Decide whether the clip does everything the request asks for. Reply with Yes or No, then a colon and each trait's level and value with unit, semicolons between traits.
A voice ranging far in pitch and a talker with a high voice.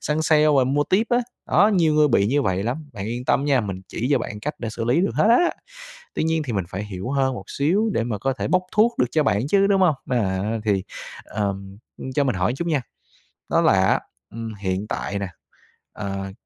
No: wide, 7.0 semitones; low, 125 Hz